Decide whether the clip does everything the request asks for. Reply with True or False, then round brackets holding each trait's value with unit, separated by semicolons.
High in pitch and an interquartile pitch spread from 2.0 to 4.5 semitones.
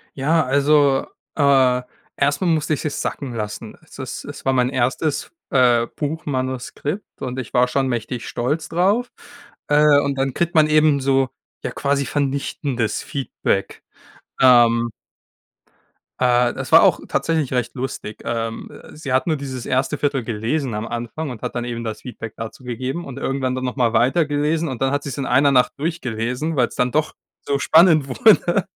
False (135 Hz; 3.2 semitones)